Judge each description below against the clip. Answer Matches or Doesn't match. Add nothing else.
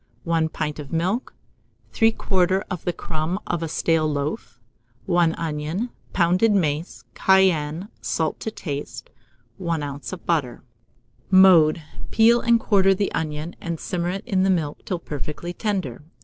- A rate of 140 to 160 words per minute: Matches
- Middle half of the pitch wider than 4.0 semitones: Doesn't match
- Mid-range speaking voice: Matches